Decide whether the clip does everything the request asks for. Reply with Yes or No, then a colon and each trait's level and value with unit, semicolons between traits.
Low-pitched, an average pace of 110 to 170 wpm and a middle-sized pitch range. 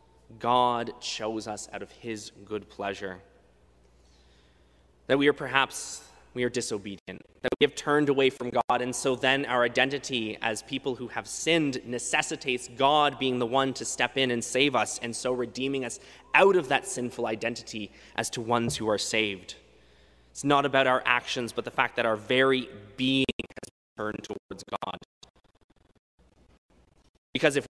Yes: low, 120 Hz; average, 165 wpm; average, 3.9 semitones